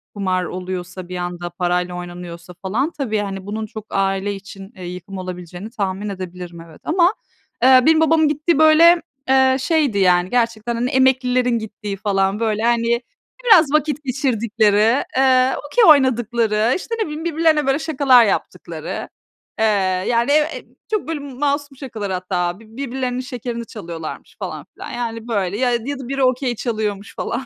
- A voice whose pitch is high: Yes, high, 230 Hz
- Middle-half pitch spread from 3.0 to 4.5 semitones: No, wide, 5.6 semitones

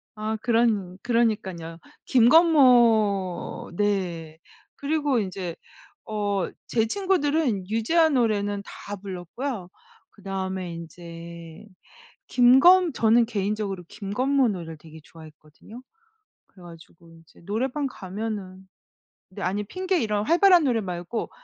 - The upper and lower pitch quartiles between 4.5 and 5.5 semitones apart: Yes, average, 5.1 semitones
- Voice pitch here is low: No, high, 205 Hz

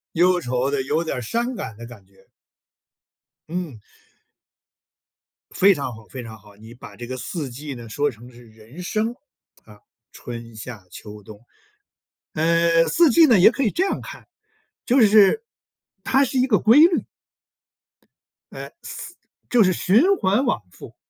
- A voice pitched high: No, medium, 155 Hz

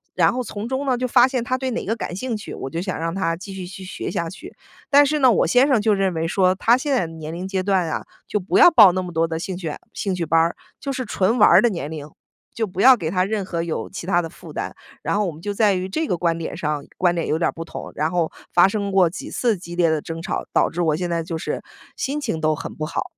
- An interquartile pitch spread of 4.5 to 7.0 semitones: Yes, average, 4.8 semitones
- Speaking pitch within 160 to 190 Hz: Yes, medium, 185 Hz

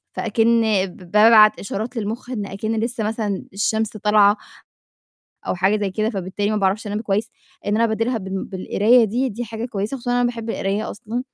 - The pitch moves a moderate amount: No, narrow, 2.2 semitones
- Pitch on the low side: No, high, 215 Hz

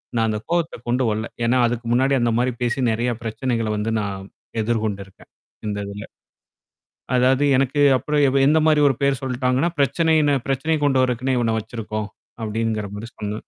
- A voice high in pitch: No, low, 120 Hz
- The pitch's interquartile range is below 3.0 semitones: No, average, 3.6 semitones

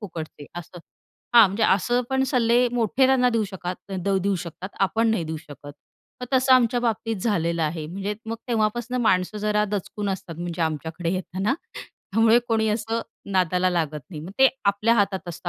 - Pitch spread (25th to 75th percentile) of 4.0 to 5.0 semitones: Yes, average, 4.6 semitones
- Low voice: No, high, 200 Hz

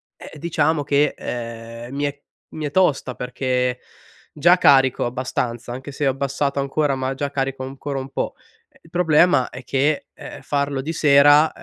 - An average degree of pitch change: No, narrow, 2.1 semitones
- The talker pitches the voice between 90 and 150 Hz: Yes, medium, 140 Hz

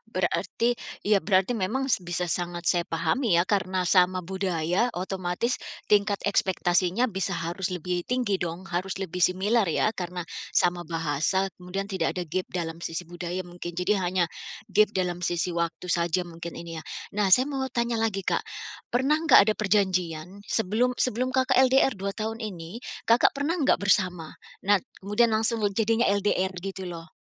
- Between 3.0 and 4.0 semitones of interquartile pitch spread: Yes, average, 3.4 semitones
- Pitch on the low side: No, medium, 185 Hz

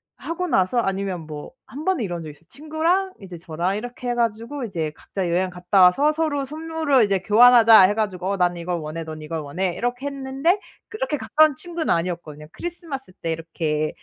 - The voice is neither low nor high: No, high, 205 Hz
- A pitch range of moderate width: No, wide, 8.6 semitones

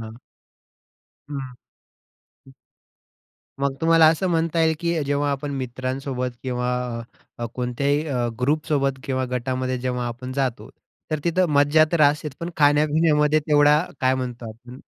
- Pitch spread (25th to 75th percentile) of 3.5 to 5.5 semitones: No, average, 3.0 semitones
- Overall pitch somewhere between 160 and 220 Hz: No, medium, 140 Hz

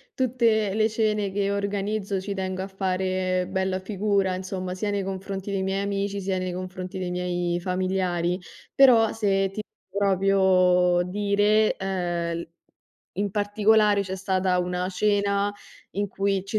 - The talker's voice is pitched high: Yes, high, 195 Hz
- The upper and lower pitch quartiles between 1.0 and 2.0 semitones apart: Yes, narrow, 1.7 semitones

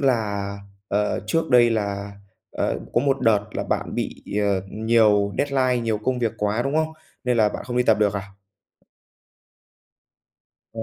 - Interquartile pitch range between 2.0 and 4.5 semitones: Yes, average, 3.3 semitones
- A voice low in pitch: Yes, low, 115 Hz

